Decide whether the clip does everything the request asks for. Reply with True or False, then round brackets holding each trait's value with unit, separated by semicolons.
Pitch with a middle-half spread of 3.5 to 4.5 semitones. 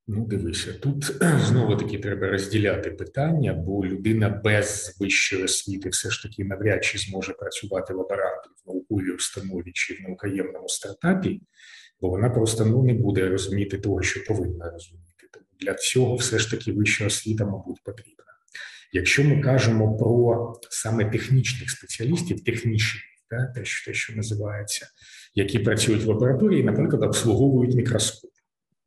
True (3.8 semitones)